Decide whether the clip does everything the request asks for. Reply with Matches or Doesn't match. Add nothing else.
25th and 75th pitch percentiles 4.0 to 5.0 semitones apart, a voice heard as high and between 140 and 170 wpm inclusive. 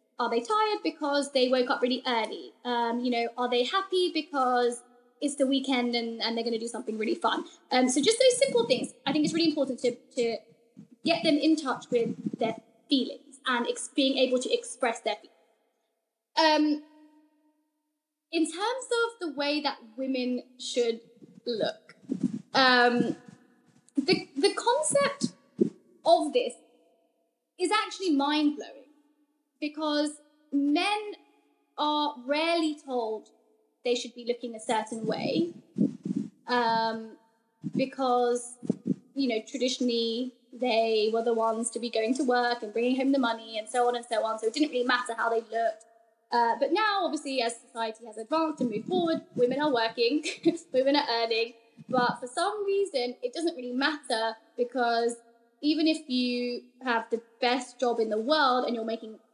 Matches